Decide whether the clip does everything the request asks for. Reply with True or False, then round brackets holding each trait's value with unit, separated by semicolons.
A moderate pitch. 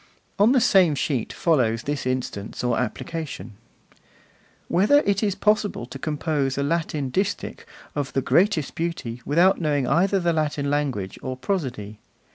True (150 Hz)